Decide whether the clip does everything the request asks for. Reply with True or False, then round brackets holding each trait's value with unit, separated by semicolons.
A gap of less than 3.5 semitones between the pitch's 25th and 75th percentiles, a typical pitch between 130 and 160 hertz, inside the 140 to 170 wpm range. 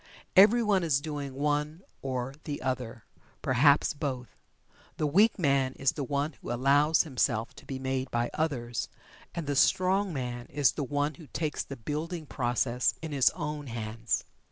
True (3.1 semitones; 140 Hz; 160 wpm)